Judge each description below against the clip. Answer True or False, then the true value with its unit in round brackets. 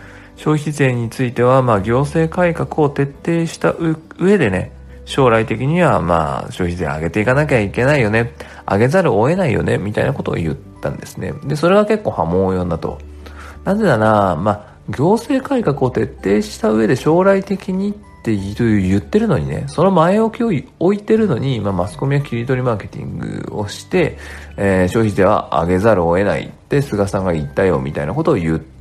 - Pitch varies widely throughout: True (9.0 semitones)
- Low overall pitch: True (115 Hz)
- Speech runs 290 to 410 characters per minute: True (375 characters per minute)